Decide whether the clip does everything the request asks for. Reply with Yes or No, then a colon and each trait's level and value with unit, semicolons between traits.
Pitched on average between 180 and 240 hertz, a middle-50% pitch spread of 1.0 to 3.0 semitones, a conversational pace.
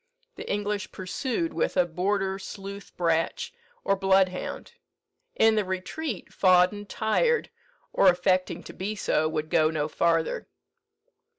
No: high, 190 Hz; average, 2.7 semitones; slow, 125 wpm